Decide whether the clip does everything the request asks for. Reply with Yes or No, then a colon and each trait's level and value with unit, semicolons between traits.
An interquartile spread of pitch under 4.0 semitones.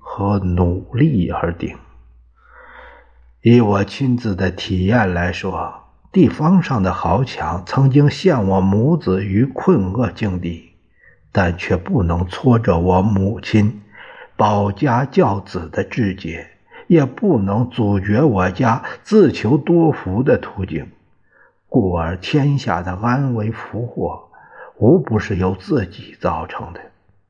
No: average, 5.3 semitones